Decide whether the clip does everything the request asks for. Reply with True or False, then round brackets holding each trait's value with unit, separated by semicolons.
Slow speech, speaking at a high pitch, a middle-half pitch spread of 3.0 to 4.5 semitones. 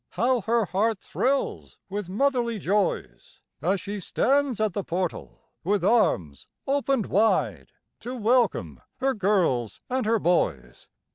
False (130 wpm; 210 Hz; 5.0 semitones)